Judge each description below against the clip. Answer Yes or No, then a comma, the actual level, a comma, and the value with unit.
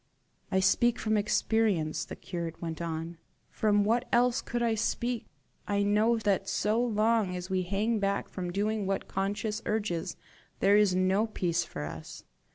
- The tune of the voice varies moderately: Yes, average, 3.3 semitones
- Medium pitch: No, high, 205 Hz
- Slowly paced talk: No, average, 165 wpm